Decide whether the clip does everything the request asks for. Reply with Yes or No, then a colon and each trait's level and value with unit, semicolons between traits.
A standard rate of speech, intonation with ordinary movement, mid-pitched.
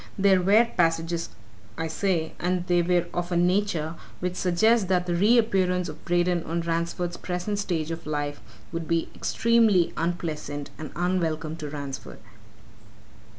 No: average, 150 wpm; narrow, 2.0 semitones; medium, 175 Hz